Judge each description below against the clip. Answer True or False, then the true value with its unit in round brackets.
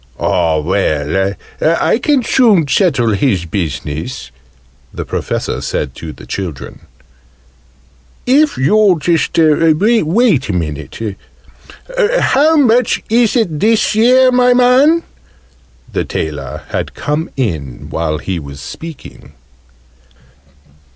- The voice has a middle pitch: True (155 Hz)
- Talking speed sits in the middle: False (105 wpm)